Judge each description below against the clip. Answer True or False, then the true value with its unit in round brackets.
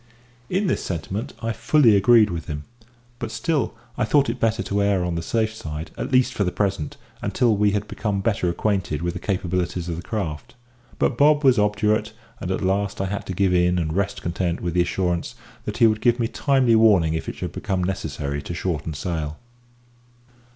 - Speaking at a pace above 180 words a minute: True (205 wpm)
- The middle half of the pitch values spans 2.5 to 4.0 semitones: False (4.5 semitones)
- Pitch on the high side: False (100 Hz)